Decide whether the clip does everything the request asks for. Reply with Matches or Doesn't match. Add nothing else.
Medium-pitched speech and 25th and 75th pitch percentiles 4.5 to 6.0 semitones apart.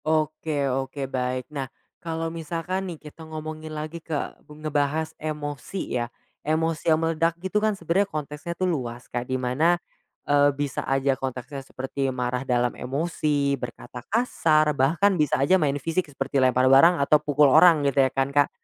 Doesn't match